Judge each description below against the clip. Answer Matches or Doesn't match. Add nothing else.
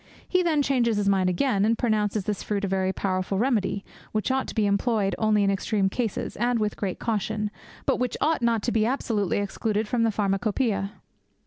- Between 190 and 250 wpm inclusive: Matches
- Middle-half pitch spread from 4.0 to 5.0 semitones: Doesn't match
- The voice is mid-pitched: Doesn't match